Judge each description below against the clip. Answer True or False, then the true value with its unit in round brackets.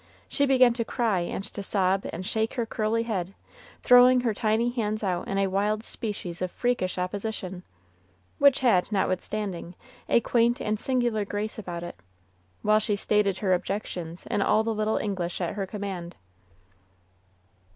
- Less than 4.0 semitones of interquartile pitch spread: True (3.5 semitones)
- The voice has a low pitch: False (210 Hz)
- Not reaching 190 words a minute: True (160 wpm)